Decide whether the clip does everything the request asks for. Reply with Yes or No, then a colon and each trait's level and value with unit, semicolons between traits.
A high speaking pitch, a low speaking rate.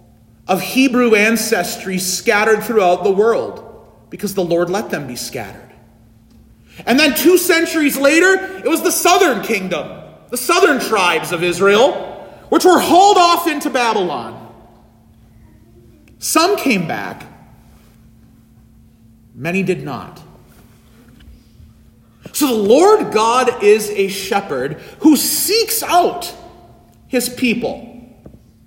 Yes: high, 220 Hz; slow, 110 wpm